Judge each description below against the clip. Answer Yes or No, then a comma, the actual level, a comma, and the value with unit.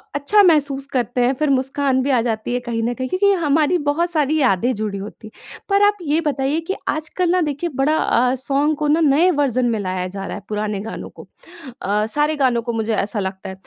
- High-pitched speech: Yes, very high, 270 Hz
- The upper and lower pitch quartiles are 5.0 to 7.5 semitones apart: Yes, average, 5.3 semitones